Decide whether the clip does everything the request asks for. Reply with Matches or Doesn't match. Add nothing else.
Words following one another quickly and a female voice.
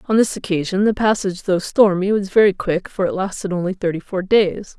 Matches